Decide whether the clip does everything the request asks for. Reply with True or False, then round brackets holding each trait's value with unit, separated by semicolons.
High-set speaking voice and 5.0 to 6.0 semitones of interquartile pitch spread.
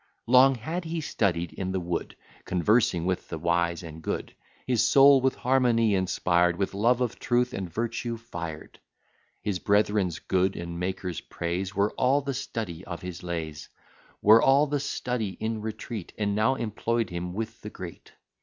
False (105 Hz; 5.4 semitones)